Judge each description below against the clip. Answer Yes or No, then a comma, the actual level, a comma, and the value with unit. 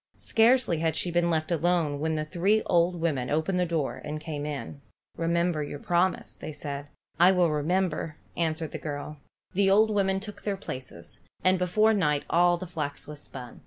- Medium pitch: Yes, medium, 170 Hz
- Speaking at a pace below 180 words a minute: No, average, 185 wpm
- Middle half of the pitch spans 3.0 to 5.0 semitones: Yes, average, 3.4 semitones